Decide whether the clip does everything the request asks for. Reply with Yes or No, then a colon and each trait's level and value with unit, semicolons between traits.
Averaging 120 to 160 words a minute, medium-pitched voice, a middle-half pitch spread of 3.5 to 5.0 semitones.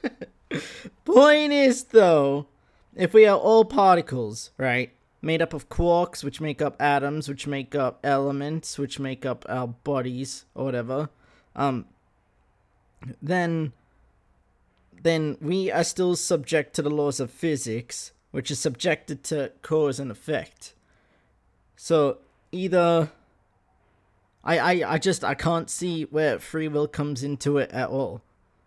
Yes: slow, 135 wpm; medium, 145 Hz; average, 4.1 semitones